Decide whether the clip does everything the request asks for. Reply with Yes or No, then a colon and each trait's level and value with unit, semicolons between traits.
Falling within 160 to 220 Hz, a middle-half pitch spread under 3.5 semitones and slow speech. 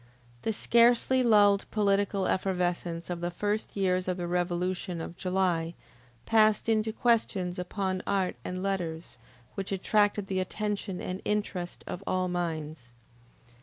Yes: medium, 185 Hz; average, 2.7 semitones; slow, 130 wpm